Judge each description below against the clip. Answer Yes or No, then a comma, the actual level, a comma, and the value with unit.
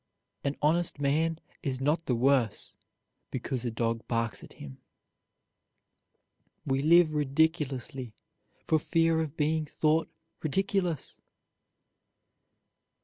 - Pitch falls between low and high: Yes, medium, 150 Hz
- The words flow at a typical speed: No, slow, 100 wpm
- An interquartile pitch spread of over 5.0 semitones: No, average, 3.7 semitones